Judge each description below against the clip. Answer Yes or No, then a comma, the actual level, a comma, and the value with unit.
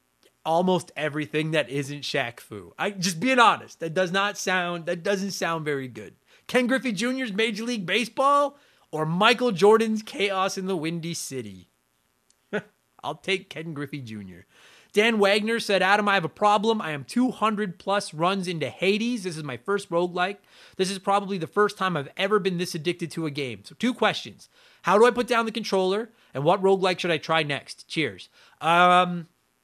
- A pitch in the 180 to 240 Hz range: Yes, high, 190 Hz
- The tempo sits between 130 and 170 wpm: No, average, 185 wpm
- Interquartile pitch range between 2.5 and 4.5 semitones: No, average, 5.0 semitones